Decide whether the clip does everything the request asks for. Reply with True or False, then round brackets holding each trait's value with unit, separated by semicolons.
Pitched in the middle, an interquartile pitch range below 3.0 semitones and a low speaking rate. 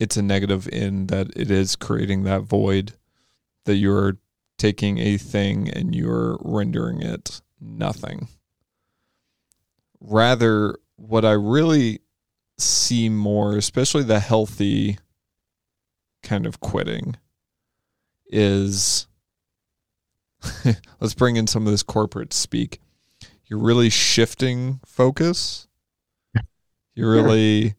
False (105 Hz; 2.4 semitones; 100 wpm)